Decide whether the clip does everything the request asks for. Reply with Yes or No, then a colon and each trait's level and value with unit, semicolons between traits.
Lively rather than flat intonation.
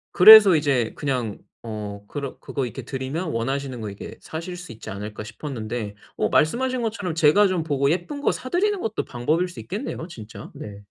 Yes: wide, 8.1 semitones